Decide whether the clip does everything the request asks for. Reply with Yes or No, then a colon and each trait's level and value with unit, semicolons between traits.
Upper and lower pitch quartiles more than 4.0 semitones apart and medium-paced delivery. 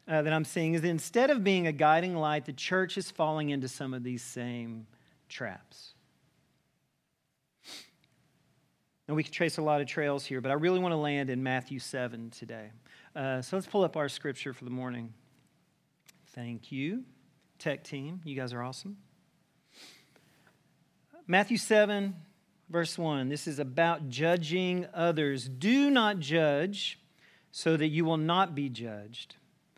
Yes: average, 4.4 semitones; average, 155 wpm